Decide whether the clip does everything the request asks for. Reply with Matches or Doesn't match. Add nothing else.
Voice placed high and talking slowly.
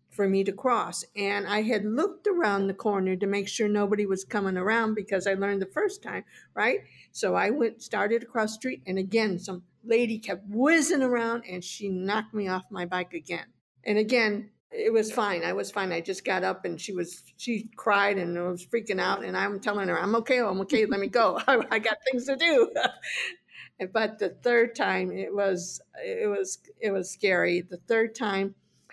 Doesn't match